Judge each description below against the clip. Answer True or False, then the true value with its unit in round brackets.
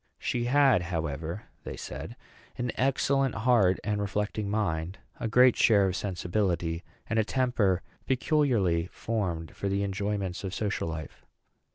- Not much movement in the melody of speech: False (4.9 semitones)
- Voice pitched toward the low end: True (100 Hz)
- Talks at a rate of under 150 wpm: True (140 wpm)